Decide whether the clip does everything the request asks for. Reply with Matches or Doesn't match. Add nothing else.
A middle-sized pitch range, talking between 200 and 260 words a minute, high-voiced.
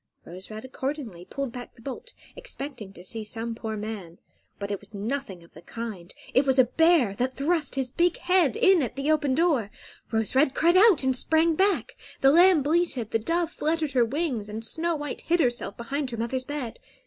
Doesn't match